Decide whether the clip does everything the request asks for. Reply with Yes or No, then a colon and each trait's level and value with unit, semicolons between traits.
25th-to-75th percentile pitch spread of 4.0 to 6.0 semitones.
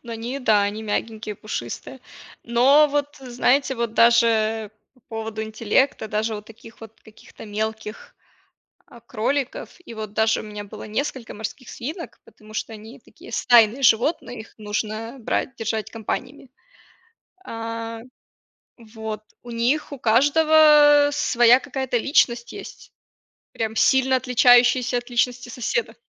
No: average, 2.9 semitones